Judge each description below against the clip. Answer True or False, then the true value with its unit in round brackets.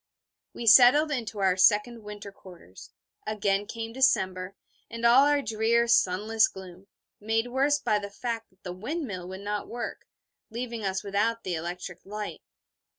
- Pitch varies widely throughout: False (3.6 semitones)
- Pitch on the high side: True (210 Hz)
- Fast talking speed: False (150 wpm)